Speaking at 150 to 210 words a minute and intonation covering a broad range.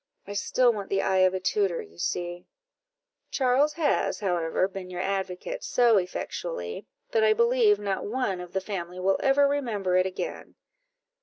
Yes: average, 165 wpm; wide, 6.8 semitones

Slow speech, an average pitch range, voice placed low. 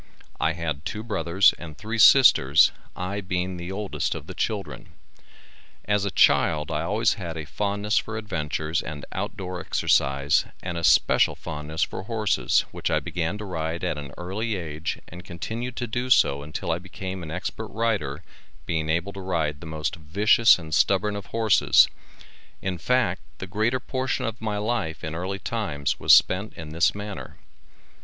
No: average, 170 wpm; average, 4.7 semitones; very low, 95 Hz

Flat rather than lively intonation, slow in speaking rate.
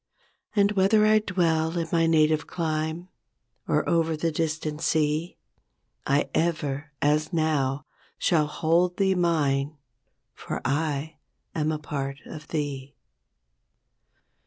Yes: narrow, 2.1 semitones; slow, 115 wpm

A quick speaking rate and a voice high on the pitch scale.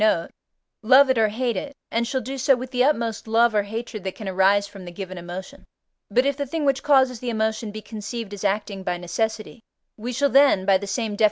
Yes: fast, 235 wpm; high, 220 Hz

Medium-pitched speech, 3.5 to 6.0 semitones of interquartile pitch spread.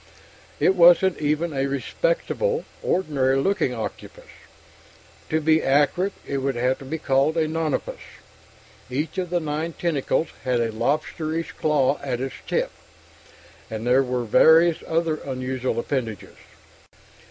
Yes: medium, 150 Hz; average, 3.9 semitones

